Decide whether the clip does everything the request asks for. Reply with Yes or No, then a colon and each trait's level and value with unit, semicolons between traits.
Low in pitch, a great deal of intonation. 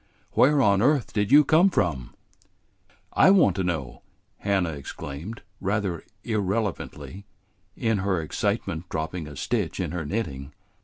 Yes: very low, 95 Hz; wide, 5.8 semitones